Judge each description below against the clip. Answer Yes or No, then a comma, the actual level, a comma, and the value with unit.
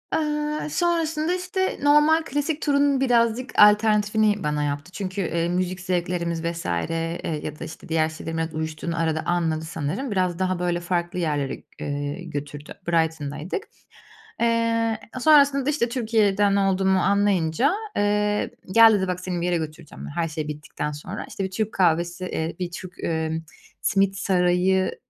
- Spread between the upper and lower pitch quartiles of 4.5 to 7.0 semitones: Yes, wide, 5.5 semitones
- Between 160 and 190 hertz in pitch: Yes, medium, 185 Hz